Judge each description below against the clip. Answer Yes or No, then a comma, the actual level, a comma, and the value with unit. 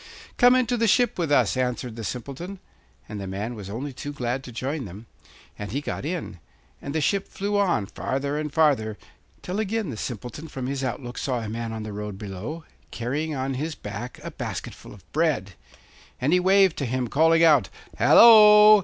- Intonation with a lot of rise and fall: Yes, wide, 6.4 semitones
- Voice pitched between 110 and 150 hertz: Yes, low, 135 Hz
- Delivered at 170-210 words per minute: Yes, average, 195 wpm